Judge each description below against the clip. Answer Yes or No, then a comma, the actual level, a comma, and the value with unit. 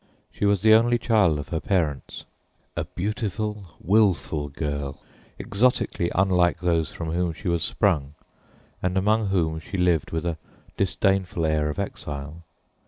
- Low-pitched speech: Yes, very low, 90 Hz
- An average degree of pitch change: Yes, average, 4.1 semitones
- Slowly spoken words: No, average, 145 wpm